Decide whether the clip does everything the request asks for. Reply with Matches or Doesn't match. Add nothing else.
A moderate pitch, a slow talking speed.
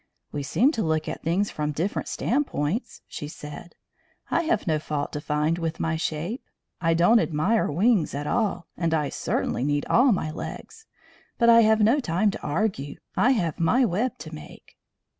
Doesn't match